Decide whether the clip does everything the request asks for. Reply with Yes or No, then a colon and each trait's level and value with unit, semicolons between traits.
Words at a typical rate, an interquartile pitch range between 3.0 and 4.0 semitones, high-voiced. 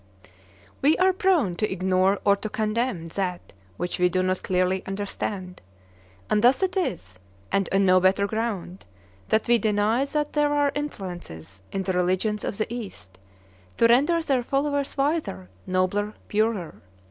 No: average, 155 wpm; wide, 5.5 semitones; high, 205 Hz